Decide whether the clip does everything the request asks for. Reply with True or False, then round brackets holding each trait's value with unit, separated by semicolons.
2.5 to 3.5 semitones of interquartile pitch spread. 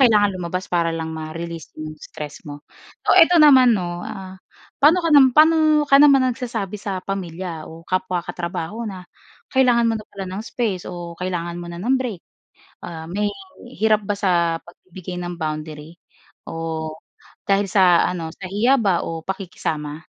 False (4.5 semitones)